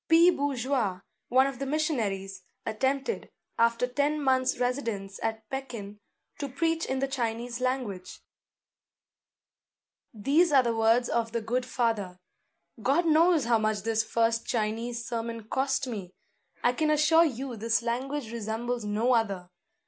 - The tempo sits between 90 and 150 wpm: Yes, average, 140 wpm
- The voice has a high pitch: Yes, high, 240 Hz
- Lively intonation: No, average, 3.5 semitones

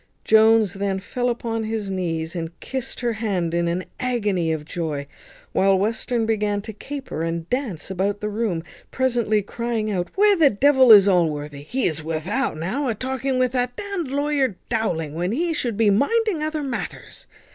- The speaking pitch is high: Yes, high, 215 Hz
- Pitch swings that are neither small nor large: No, wide, 6.1 semitones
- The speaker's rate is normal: Yes, average, 180 wpm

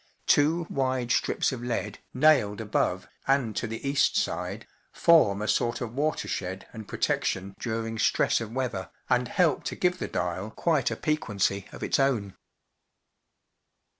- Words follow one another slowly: No, average, 155 wpm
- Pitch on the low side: Yes, low, 115 Hz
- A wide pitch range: No, average, 5.0 semitones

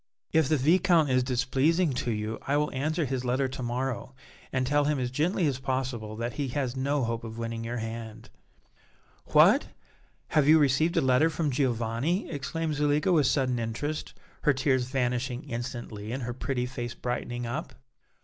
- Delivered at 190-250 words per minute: No, average, 175 wpm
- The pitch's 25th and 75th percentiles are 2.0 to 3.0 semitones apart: No, average, 3.4 semitones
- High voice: No, low, 130 Hz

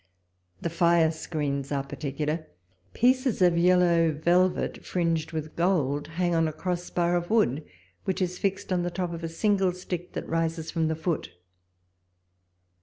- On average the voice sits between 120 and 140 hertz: No, medium, 170 Hz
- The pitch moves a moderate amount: No, narrow, 2.3 semitones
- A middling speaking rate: Yes, average, 160 wpm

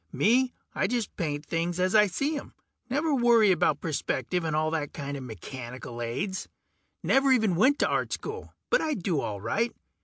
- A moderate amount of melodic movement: No, wide, 8.8 semitones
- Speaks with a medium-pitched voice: Yes, medium, 180 Hz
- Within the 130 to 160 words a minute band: No, average, 180 wpm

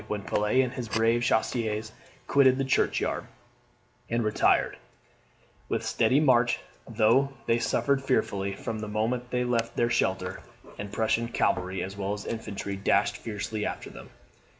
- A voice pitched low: Yes, low, 115 Hz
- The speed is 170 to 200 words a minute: No, average, 150 wpm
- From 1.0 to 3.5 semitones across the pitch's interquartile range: Yes, average, 2.8 semitones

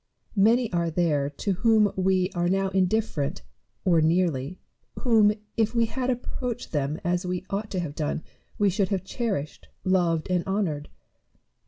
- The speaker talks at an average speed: Yes, average, 155 wpm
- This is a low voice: No, medium, 185 Hz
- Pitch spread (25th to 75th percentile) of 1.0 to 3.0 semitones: No, average, 4.1 semitones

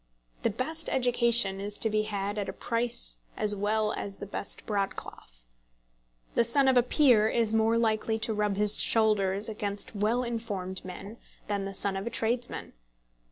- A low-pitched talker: No, high, 215 Hz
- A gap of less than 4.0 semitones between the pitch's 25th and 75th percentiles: Yes, narrow, 2.6 semitones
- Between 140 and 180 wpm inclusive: Yes, average, 170 wpm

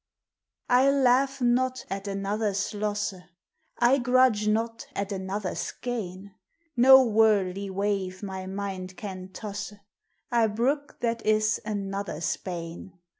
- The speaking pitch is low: No, high, 210 Hz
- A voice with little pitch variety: No, average, 3.6 semitones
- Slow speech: Yes, slow, 115 wpm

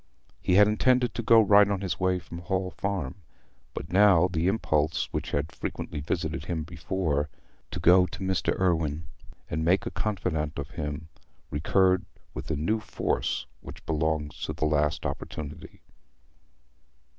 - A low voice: Yes, very low, 85 Hz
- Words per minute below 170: Yes, average, 150 wpm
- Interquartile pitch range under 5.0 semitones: Yes, average, 3.9 semitones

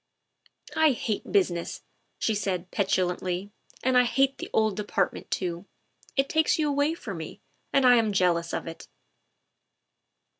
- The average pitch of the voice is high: Yes, high, 205 Hz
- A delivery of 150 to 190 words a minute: Yes, average, 155 wpm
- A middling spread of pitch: No, wide, 6.9 semitones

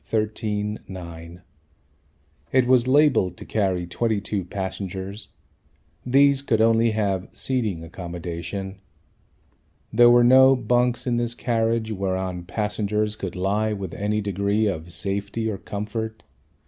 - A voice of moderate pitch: No, low, 105 Hz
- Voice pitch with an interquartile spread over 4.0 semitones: No, average, 3.4 semitones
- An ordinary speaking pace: No, slow, 120 wpm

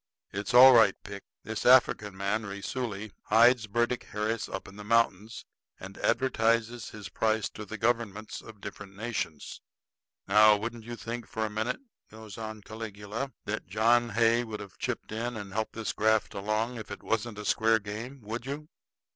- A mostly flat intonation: Yes, narrow, 2.1 semitones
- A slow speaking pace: No, average, 170 wpm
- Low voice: Yes, low, 110 Hz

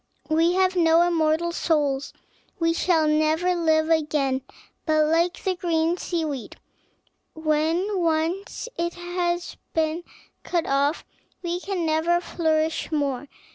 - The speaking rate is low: Yes, slow, 125 wpm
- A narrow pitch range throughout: Yes, narrow, 1.9 semitones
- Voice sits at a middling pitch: No, very high, 325 Hz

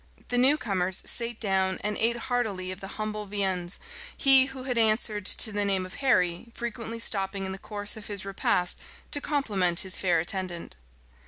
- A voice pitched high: Yes, high, 205 Hz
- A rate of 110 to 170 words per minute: No, average, 180 wpm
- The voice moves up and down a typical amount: Yes, average, 3.7 semitones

